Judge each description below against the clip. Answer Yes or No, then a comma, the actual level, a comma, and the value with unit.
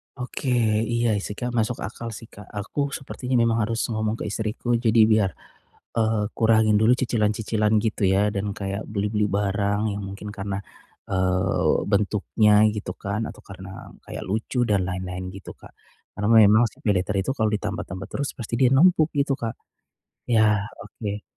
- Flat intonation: Yes, narrow, 2.3 semitones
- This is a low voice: Yes, low, 105 Hz